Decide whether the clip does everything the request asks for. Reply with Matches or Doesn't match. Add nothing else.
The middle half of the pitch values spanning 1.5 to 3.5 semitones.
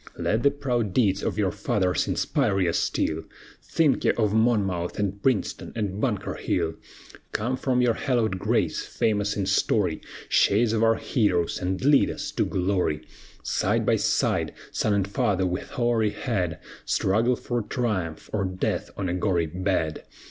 Doesn't match